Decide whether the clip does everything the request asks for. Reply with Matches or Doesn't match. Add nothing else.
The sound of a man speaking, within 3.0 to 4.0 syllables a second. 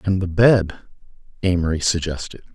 Doesn't match